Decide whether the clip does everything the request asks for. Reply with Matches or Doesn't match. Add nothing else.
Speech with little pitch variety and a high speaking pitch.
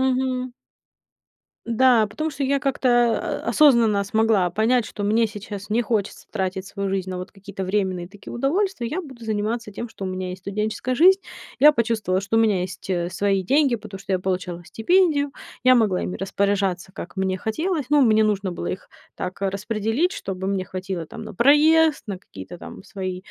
Doesn't match